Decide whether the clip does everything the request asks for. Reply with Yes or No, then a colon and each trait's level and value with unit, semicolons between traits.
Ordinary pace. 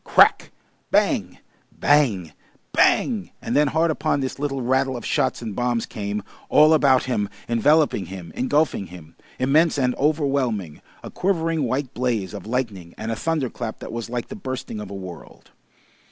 Yes: average, 165 wpm